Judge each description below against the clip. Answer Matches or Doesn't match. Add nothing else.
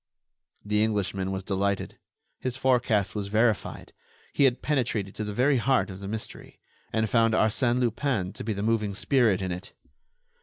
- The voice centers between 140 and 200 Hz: Doesn't match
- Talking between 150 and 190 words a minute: Matches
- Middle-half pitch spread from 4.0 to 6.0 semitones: Doesn't match